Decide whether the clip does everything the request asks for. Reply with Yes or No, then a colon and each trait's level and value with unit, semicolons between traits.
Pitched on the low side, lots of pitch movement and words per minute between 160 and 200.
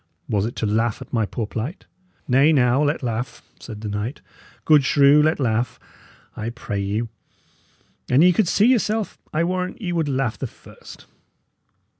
Yes: low, 130 Hz; wide, 6.0 semitones; average, 170 wpm